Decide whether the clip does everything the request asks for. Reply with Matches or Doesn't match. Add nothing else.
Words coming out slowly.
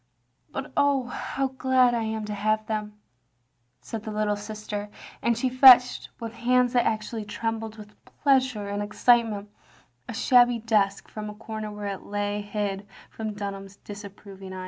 Doesn't match